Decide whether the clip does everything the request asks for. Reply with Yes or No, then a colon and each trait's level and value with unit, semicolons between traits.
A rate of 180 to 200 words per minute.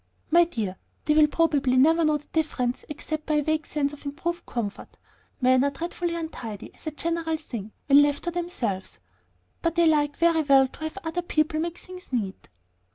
Yes: average, 190 wpm